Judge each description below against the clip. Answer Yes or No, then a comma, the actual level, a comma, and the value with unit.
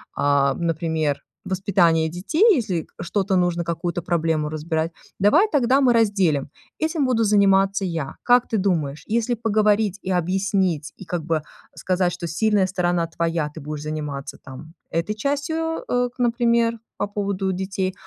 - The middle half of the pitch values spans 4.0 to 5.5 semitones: Yes, average, 4.9 semitones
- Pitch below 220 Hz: Yes, medium, 185 Hz